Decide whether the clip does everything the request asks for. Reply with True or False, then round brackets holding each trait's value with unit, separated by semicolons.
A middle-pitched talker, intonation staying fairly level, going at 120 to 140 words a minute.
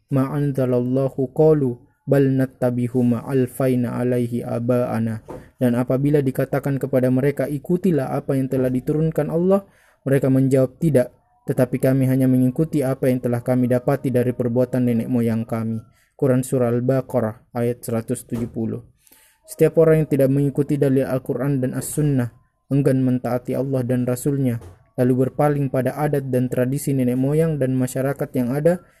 False (130 Hz; 2.1 semitones; 135 wpm)